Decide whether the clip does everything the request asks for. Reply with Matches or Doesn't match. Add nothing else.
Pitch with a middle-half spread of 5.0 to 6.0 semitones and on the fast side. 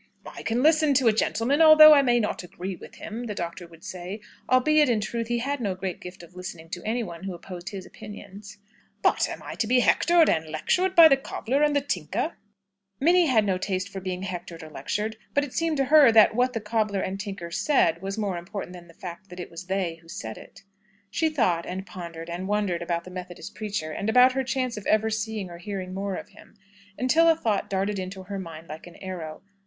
Matches